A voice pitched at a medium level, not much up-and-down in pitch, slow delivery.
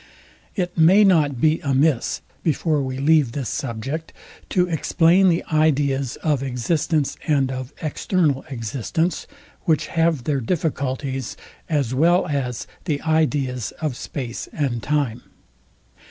No: medium, 145 Hz; average, 3.6 semitones; slow, 125 wpm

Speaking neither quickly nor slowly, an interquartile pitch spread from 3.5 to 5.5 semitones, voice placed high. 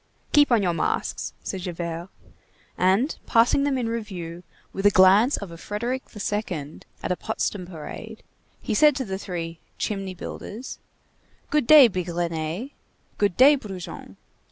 Yes: average, 145 wpm; average, 5.1 semitones; high, 200 Hz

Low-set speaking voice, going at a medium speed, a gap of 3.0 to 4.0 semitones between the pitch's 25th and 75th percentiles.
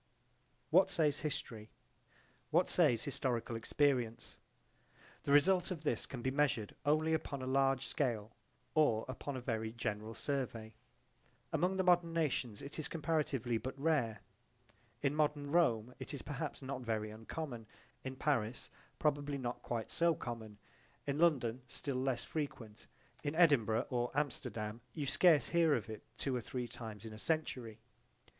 No: low, 130 Hz; average, 150 wpm; average, 4.6 semitones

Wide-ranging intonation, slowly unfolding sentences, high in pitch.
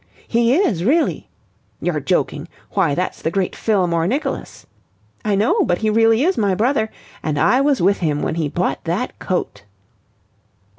No: wide, 5.7 semitones; average, 160 wpm; high, 200 Hz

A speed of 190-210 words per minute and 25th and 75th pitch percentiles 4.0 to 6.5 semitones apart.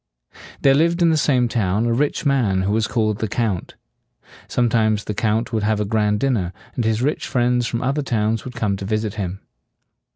No: average, 200 wpm; average, 3.0 semitones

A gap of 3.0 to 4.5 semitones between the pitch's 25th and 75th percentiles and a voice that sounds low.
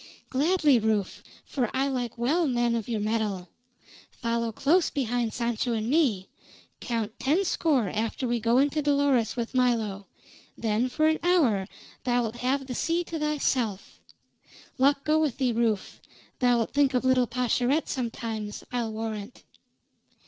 No: average, 3.8 semitones; high, 245 Hz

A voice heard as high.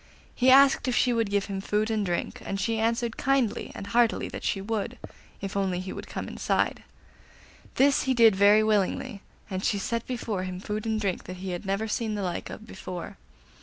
Yes: high, 210 Hz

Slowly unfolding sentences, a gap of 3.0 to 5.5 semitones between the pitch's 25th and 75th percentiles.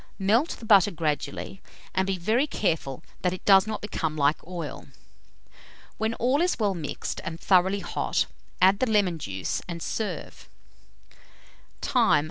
No: average, 145 wpm; average, 4.4 semitones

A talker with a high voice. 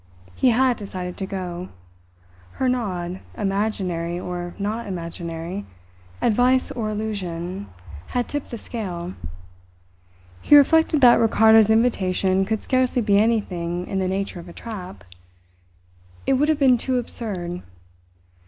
Yes: high, 200 Hz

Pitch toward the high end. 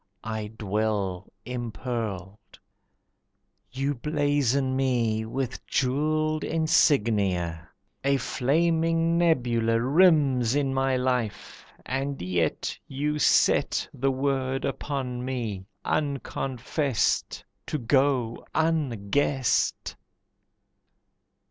No: low, 130 Hz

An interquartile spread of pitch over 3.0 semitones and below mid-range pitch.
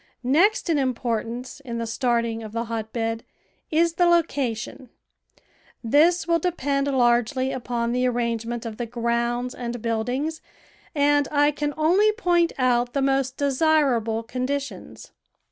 No: average, 3.8 semitones; very high, 255 Hz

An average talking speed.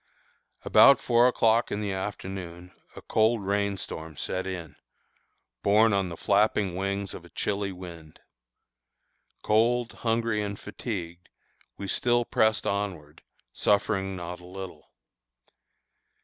No: slow, 120 wpm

